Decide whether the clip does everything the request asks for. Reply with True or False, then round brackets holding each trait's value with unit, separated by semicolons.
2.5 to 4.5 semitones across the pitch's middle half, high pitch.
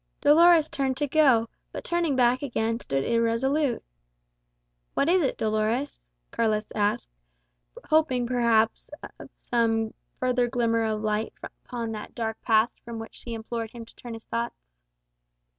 True (2.8 semitones; 235 Hz)